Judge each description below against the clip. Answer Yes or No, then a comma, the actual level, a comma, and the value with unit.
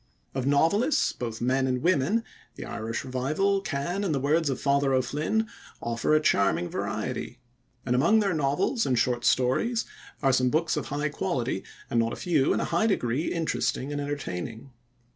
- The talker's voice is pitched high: No, medium, 140 Hz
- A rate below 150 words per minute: No, average, 175 wpm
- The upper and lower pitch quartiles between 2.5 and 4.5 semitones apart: No, average, 4.9 semitones